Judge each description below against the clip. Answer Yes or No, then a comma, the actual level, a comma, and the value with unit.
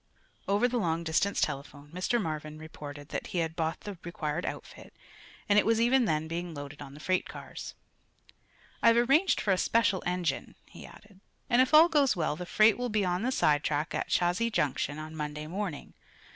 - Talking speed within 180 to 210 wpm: Yes, average, 190 wpm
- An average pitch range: No, wide, 6.1 semitones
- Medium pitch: Yes, medium, 175 Hz